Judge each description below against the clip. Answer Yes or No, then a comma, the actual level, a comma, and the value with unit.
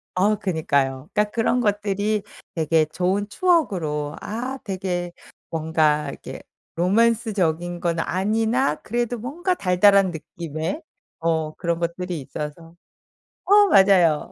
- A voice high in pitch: No, medium, 180 Hz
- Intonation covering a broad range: No, average, 4.9 semitones